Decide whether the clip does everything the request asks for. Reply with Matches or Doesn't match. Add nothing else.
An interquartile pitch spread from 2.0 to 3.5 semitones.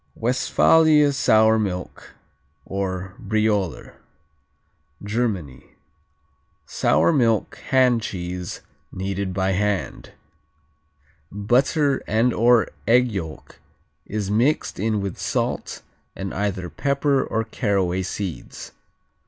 Doesn't match